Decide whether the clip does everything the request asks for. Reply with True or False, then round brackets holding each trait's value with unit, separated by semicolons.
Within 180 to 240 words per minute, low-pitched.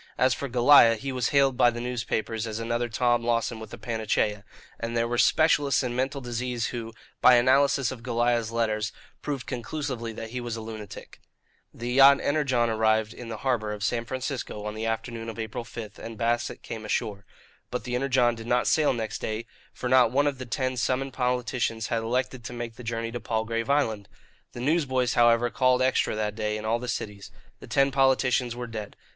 True (200 wpm; 120 Hz)